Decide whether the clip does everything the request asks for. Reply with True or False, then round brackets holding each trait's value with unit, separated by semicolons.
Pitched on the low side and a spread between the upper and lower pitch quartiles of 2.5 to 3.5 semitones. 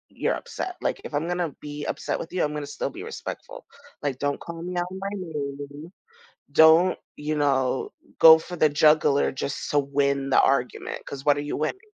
False (150 Hz; 2.8 semitones)